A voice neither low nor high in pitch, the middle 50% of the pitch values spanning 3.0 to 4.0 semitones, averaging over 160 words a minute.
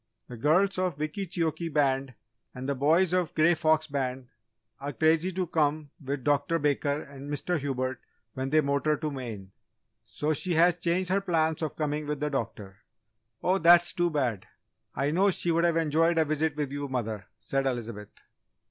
Yes: medium, 150 Hz; average, 3.5 semitones; average, 180 wpm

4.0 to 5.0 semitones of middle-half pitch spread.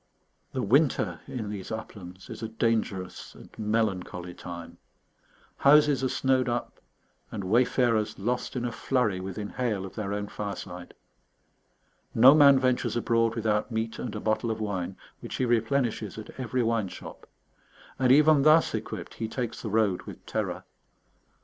No: average, 3.6 semitones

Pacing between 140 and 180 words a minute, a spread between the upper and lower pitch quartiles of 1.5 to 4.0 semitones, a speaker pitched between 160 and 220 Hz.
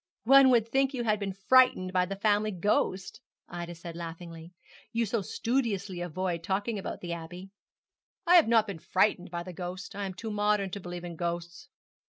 No: average, 190 wpm; average, 3.6 semitones; high, 190 Hz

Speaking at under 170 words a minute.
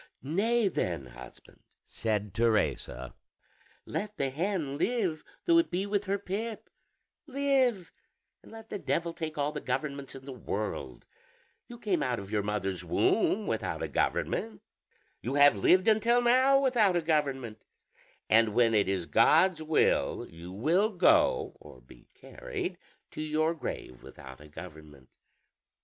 Yes: average, 145 wpm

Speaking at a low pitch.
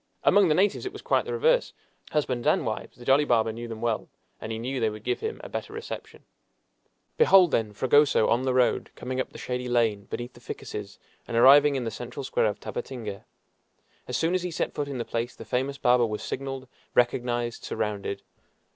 Yes: low, 125 Hz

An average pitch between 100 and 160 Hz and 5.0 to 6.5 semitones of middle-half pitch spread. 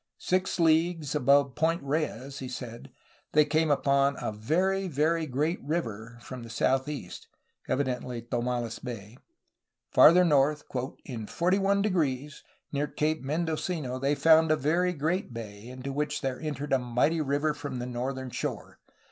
No: medium, 140 Hz; average, 4.0 semitones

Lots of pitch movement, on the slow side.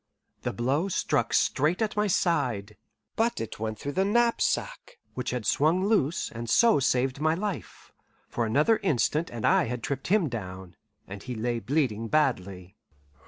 No: wide, 8.1 semitones; average, 165 wpm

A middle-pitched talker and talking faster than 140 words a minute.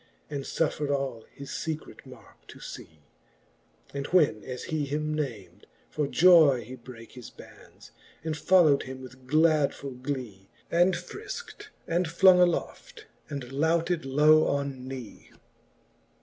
No: medium, 145 Hz; slow, 135 wpm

